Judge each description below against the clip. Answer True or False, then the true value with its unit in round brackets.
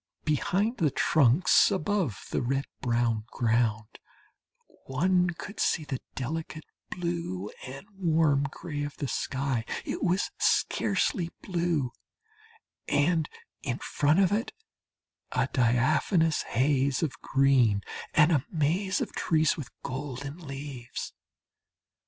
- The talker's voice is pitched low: False (145 Hz)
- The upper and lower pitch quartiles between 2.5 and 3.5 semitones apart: False (4.8 semitones)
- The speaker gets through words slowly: True (115 wpm)